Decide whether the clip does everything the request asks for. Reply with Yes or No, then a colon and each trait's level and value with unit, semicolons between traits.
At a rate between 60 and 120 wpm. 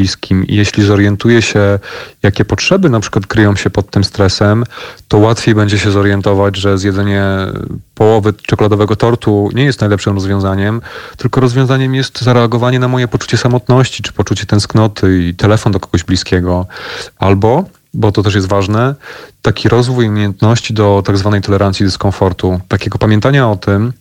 No: average, 150 wpm